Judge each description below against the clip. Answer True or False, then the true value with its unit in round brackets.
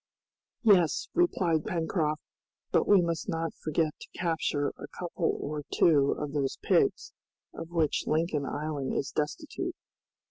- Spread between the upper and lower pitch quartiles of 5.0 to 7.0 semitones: False (2.4 semitones)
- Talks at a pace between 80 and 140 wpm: True (135 wpm)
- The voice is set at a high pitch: False (160 Hz)